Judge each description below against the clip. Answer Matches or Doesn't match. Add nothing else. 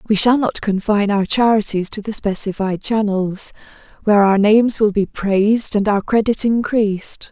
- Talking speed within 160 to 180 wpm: Matches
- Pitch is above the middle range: Matches